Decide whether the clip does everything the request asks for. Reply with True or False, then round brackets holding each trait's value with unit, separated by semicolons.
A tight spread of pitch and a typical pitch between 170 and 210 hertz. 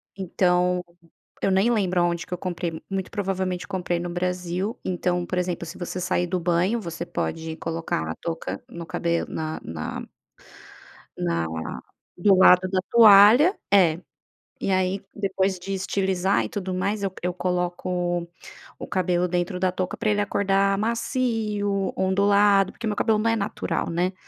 True (2.1 semitones; 185 Hz)